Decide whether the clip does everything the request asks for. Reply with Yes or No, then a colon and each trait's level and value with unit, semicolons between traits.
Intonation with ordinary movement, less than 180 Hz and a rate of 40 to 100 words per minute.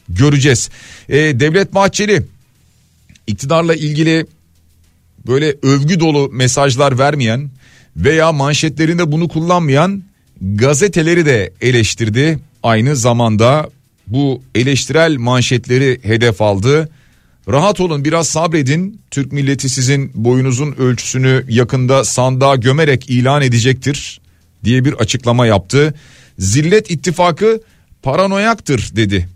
Yes: average, 4.3 semitones; low, 135 Hz; slow, 95 wpm